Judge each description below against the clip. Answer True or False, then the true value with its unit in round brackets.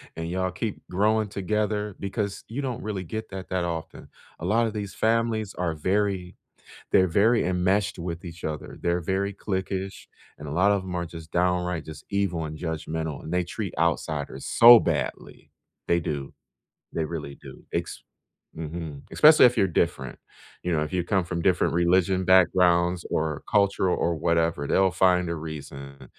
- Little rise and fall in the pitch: False (3.3 semitones)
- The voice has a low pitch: True (90 Hz)